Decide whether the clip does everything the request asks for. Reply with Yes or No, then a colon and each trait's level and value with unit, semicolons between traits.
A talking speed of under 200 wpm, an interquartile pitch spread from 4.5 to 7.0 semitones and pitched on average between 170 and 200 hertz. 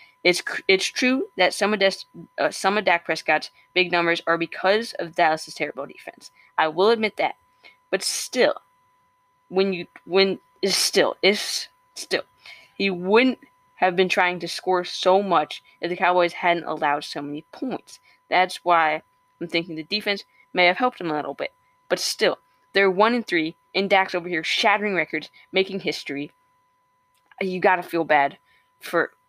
Yes: average, 170 wpm; average, 4.8 semitones; high, 190 Hz